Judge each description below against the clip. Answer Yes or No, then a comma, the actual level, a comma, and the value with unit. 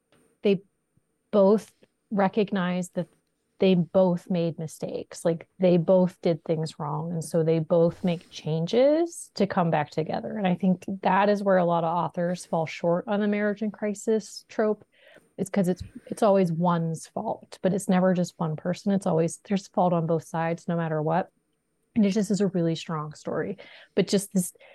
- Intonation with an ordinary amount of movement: Yes, average, 3.2 semitones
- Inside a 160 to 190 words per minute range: Yes, average, 185 wpm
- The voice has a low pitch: No, medium, 180 Hz